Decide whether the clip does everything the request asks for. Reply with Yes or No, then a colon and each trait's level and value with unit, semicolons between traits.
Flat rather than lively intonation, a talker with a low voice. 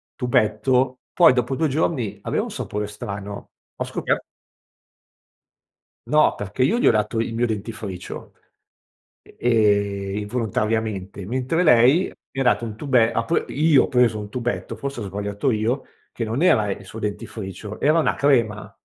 No: average, 3.9 semitones; low, 115 Hz